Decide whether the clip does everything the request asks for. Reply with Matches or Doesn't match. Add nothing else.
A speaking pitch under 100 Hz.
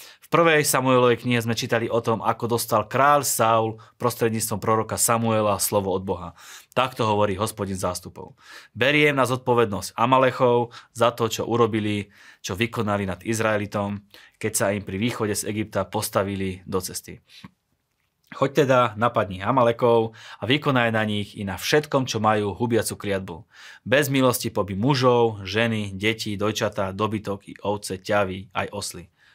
Doesn't match